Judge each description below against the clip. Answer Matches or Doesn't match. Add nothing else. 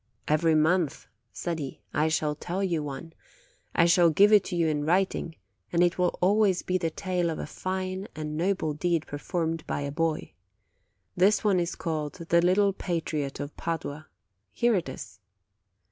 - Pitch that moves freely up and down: Doesn't match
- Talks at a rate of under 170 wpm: Doesn't match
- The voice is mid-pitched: Matches